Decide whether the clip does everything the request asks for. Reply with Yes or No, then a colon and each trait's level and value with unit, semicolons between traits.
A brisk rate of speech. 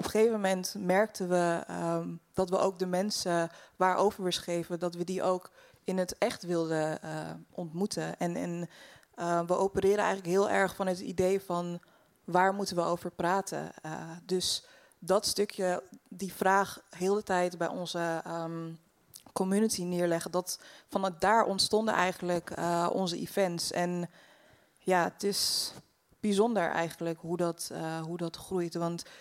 No: average, 155 wpm